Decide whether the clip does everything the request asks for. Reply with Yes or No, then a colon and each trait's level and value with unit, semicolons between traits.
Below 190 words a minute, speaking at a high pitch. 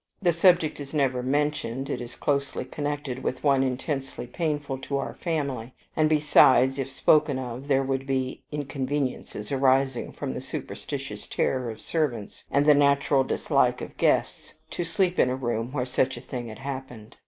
No: average, 170 wpm; low, 135 Hz